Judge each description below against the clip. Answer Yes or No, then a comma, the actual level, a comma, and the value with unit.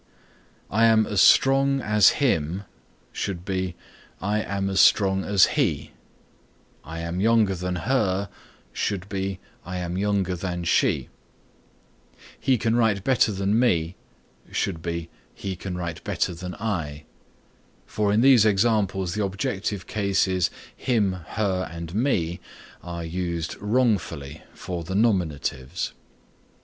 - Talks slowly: Yes, slow, 130 wpm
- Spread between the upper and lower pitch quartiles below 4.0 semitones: Yes, average, 3.5 semitones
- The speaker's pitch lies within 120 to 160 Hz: No, very low, 95 Hz